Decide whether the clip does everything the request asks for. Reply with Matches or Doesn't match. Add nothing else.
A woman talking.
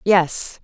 Matches